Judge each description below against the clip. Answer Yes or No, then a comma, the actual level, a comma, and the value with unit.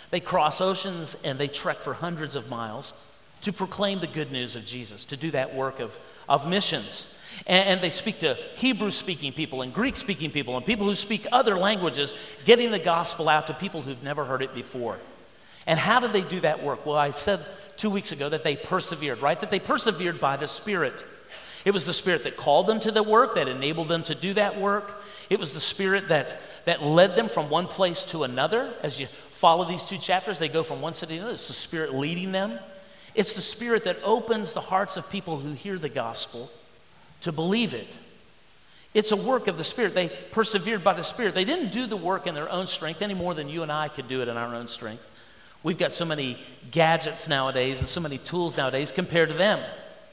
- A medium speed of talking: No, fast, 225 wpm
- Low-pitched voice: No, medium, 175 Hz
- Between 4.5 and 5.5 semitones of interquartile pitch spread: Yes, average, 5.2 semitones